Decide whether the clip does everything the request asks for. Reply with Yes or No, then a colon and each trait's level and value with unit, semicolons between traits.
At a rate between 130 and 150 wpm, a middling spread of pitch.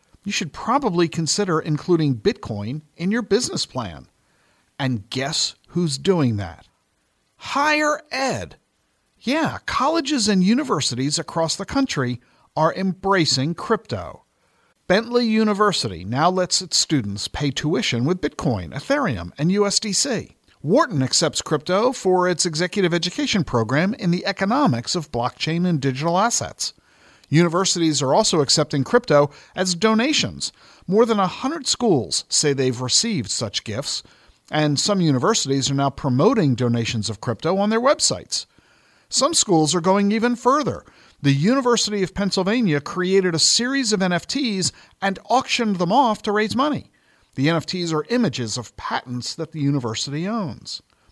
No: slow, 135 wpm; wide, 7.0 semitones